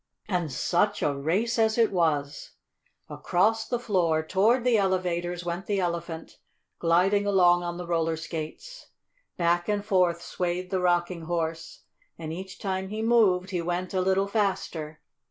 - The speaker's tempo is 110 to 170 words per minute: Yes, average, 155 wpm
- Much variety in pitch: No, average, 2.9 semitones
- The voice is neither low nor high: Yes, medium, 180 Hz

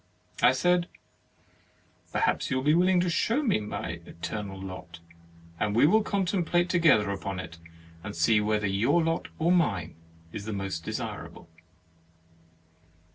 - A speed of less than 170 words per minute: Yes, average, 140 wpm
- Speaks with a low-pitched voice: Yes, low, 110 Hz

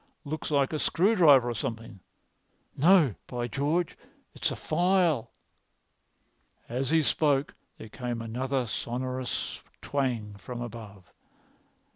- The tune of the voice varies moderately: Yes, average, 4.4 semitones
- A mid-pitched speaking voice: No, low, 130 Hz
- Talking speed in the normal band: No, slow, 110 wpm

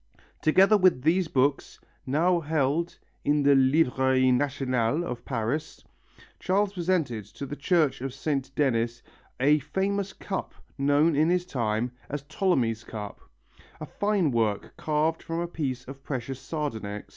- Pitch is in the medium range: Yes, medium, 145 Hz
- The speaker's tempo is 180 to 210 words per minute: No, average, 140 wpm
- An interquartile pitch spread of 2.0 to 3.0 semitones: No, average, 4.5 semitones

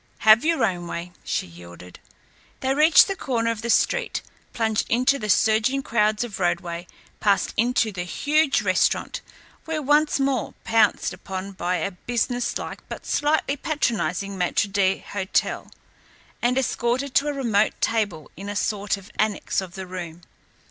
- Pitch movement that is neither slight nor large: No, wide, 5.7 semitones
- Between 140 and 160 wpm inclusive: Yes, average, 150 wpm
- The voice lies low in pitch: No, high, 220 Hz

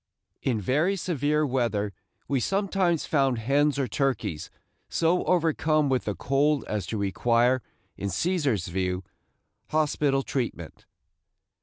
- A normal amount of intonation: No, wide, 5.7 semitones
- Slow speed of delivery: Yes, slow, 120 wpm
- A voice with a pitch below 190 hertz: Yes, low, 135 Hz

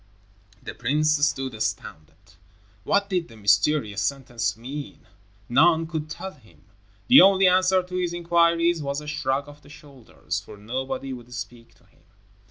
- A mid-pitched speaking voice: Yes, medium, 145 Hz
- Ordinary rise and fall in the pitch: No, wide, 5.7 semitones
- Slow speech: No, average, 155 wpm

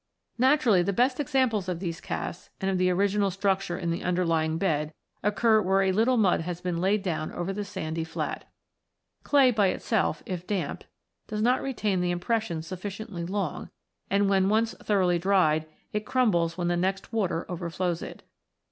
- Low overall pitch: No, high, 190 Hz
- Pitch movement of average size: Yes, average, 3.3 semitones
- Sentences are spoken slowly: No, average, 175 wpm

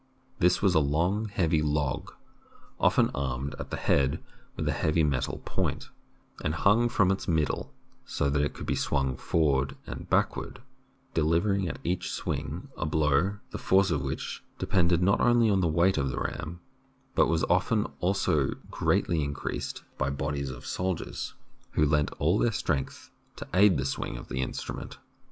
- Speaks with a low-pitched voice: Yes, very low, 80 Hz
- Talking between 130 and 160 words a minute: No, average, 175 wpm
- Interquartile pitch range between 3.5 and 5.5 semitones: Yes, average, 4.9 semitones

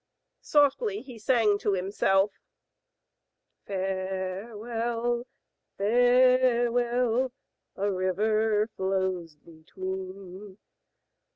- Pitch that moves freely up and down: No, average, 4.2 semitones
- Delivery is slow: Yes, slow, 60 wpm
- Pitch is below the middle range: No, high, 210 Hz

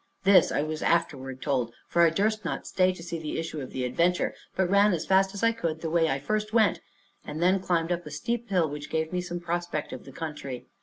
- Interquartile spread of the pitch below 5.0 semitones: Yes, average, 3.8 semitones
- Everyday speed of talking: No, fast, 245 wpm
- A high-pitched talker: No, medium, 170 Hz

